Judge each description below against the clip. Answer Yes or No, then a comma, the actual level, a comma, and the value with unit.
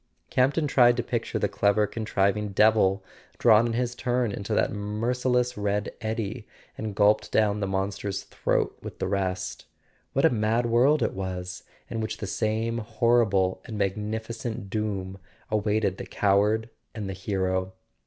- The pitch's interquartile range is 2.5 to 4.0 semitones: Yes, average, 2.8 semitones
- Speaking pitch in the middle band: No, low, 105 Hz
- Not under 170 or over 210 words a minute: No, average, 155 wpm